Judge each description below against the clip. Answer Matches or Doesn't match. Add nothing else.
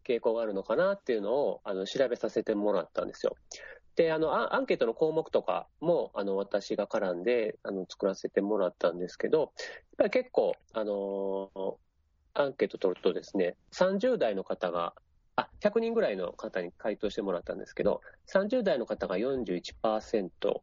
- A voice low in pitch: Doesn't match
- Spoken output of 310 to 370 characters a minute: Matches